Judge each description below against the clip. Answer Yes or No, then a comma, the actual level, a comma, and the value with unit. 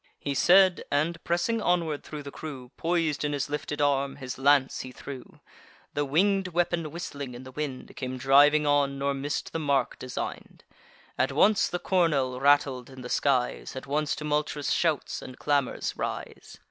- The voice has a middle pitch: Yes, medium, 145 Hz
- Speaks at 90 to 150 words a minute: No, average, 170 wpm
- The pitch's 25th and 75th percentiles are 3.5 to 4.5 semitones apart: No, average, 2.8 semitones